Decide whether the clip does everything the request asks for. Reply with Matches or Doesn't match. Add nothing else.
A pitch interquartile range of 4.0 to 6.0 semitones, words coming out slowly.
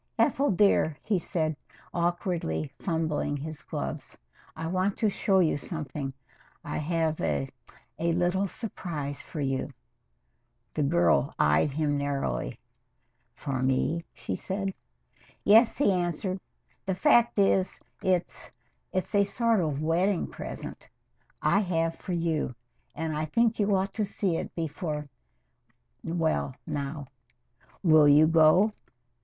Matches